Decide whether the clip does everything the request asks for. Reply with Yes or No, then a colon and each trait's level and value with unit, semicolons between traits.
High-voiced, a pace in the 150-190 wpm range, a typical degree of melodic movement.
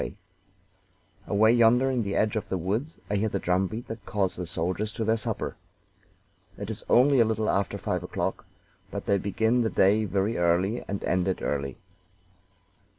No: low, 105 Hz; average, 180 wpm; average, 3.0 semitones